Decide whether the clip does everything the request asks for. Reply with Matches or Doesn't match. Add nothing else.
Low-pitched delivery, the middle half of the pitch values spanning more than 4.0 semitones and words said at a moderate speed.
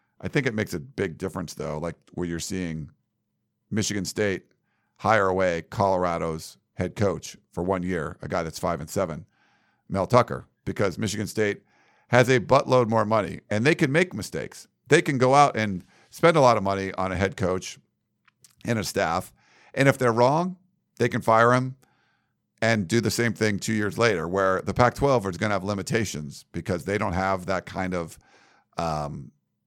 Matches